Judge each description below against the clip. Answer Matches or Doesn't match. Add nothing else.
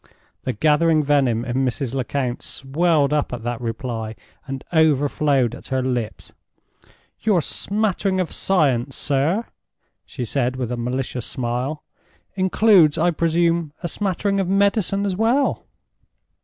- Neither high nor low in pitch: Matches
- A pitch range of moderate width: Doesn't match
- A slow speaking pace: Matches